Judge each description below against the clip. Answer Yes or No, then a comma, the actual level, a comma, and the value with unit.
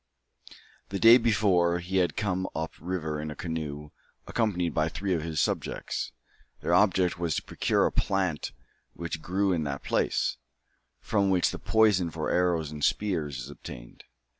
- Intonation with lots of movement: No, average, 3.6 semitones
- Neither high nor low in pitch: No, very low, 85 Hz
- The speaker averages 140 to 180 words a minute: Yes, average, 165 wpm